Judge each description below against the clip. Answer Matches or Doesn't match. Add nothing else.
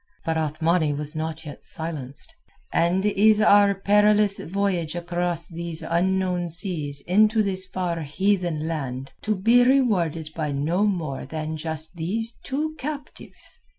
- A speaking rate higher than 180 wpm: Doesn't match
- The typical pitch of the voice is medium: Matches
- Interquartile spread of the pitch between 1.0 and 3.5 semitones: Doesn't match